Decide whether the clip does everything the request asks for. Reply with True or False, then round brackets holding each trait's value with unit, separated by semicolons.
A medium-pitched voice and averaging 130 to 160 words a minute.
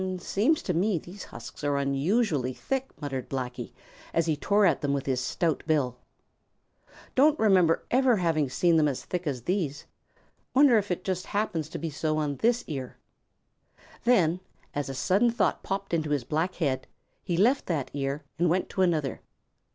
False (165 Hz; 175 wpm)